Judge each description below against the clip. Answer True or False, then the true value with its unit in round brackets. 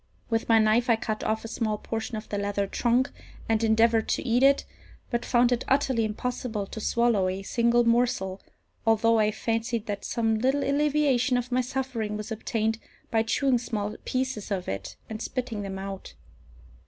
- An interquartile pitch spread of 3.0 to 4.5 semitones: False (2.5 semitones)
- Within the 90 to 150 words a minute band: False (180 wpm)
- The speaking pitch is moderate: False (225 Hz)